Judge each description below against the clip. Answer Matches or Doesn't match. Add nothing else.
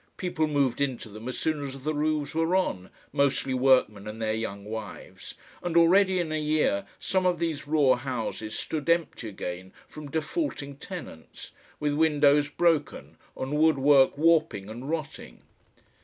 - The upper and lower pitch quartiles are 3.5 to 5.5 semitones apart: Matches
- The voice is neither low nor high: Matches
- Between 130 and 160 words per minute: Matches